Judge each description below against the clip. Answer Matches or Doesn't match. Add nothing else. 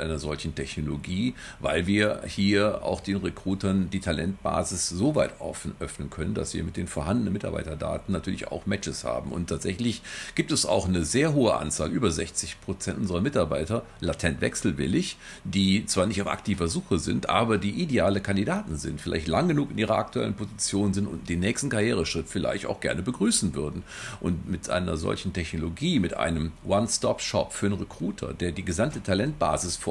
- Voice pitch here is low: Matches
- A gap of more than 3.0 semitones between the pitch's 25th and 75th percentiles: Matches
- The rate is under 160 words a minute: Doesn't match